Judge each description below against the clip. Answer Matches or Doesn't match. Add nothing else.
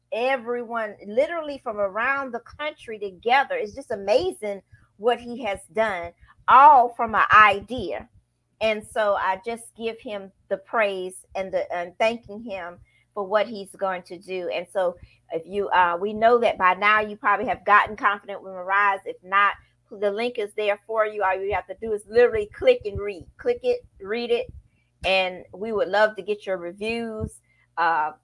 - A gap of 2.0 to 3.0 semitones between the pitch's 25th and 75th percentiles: Doesn't match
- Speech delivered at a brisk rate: Doesn't match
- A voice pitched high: Matches